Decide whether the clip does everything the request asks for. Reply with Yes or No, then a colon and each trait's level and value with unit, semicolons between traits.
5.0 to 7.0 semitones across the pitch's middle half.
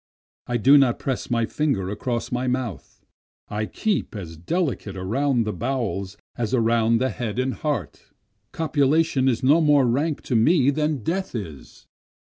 No: average, 4.6 semitones